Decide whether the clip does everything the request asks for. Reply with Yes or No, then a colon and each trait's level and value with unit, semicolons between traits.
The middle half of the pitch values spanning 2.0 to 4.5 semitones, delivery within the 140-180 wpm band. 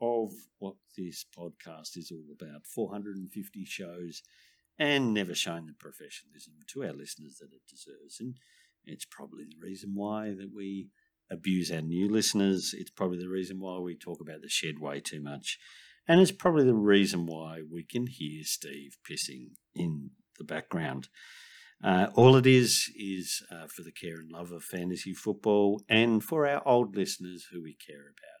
Yes: average, 4.1 semitones; average, 175 wpm